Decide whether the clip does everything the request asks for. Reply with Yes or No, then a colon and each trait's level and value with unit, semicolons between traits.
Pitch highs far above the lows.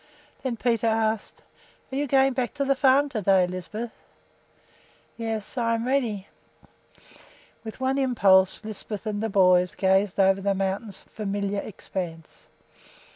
No: average, 3.9 semitones